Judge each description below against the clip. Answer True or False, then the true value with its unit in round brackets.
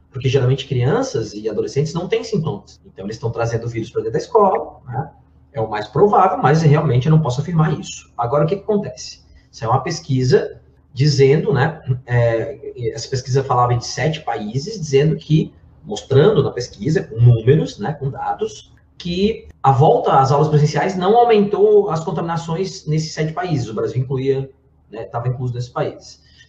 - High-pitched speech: False (140 Hz)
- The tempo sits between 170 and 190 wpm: True (175 wpm)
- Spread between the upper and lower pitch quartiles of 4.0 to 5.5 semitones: True (5.1 semitones)